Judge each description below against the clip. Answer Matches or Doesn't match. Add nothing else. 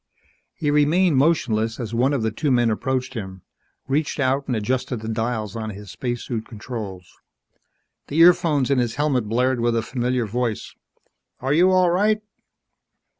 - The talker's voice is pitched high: Doesn't match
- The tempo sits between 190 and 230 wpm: Doesn't match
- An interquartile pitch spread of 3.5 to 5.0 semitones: Matches